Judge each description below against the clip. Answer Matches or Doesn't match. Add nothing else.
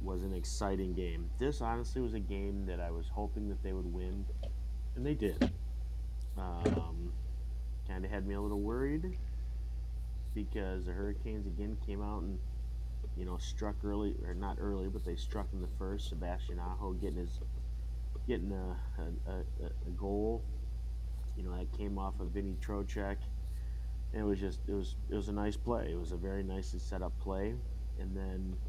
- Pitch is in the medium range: Doesn't match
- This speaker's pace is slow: Doesn't match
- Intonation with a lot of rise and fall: Matches